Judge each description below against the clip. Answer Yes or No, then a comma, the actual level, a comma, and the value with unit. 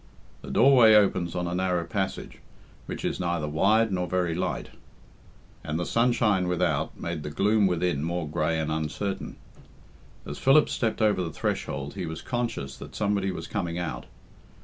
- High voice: No, very low, 90 Hz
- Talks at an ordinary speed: Yes, average, 165 wpm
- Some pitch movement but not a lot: Yes, average, 4.0 semitones